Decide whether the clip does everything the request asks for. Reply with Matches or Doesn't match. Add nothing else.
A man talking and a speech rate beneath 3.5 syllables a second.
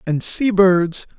Matches